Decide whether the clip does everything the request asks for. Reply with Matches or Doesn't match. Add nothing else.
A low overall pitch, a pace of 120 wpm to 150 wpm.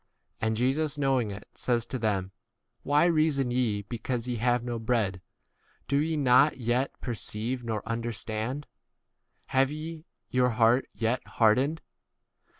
Matches